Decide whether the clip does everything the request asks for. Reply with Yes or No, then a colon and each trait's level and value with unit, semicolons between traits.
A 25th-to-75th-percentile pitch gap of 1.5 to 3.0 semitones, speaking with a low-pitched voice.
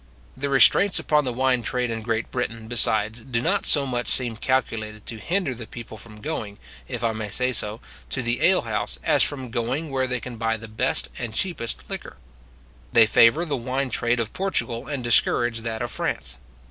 Yes: average, 2.7 semitones; low, 120 Hz